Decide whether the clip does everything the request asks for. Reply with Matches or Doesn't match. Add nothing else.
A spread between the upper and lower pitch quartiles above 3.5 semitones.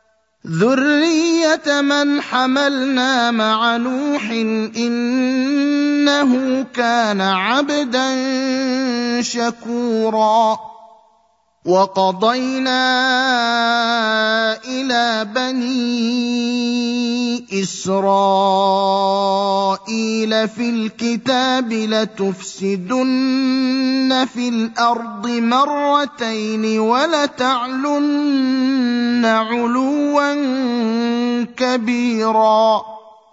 Doesn't match